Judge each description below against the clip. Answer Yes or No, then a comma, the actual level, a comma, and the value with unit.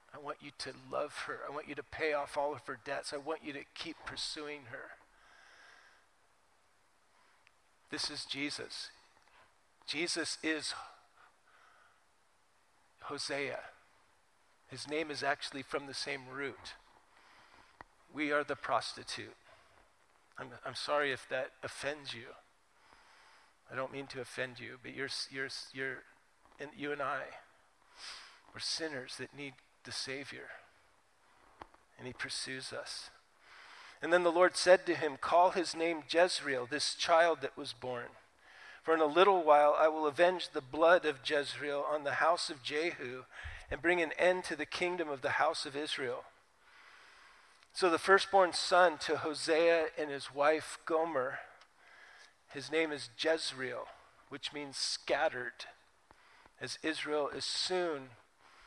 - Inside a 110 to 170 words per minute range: Yes, average, 140 wpm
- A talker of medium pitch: Yes, medium, 150 Hz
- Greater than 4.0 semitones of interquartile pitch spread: No, average, 3.1 semitones